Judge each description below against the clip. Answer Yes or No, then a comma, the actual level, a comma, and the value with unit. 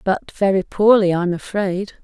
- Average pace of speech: Yes, average, 145 wpm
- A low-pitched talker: No, high, 190 Hz